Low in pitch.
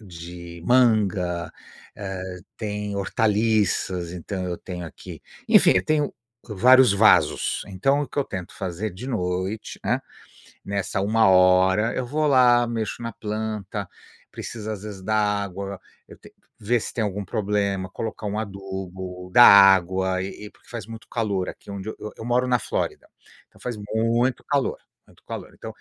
Yes: low, 100 Hz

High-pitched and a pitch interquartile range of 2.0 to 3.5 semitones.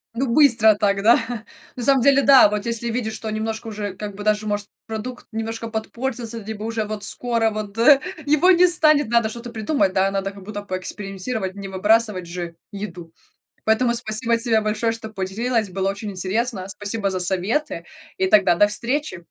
Yes: high, 220 Hz; average, 2.8 semitones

